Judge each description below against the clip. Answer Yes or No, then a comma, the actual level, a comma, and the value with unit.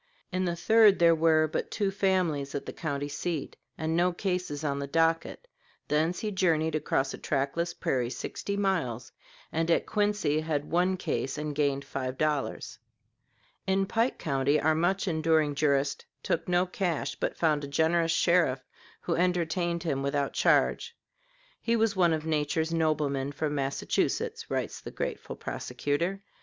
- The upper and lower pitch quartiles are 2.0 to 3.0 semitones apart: No, average, 3.8 semitones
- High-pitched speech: No, medium, 160 Hz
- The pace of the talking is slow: No, average, 155 wpm